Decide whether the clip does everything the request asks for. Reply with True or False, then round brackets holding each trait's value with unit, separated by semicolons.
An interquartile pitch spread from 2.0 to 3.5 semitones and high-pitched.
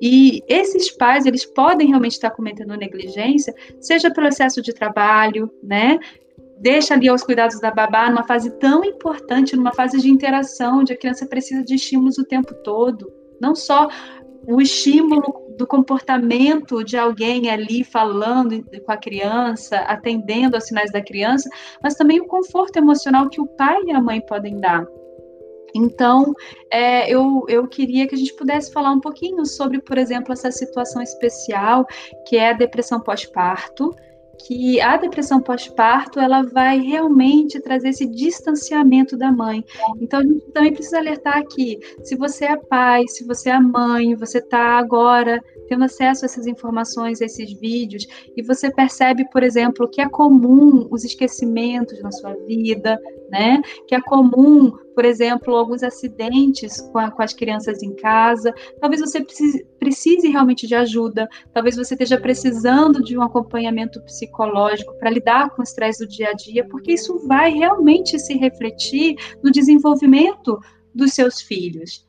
True (2.9 semitones; 255 Hz)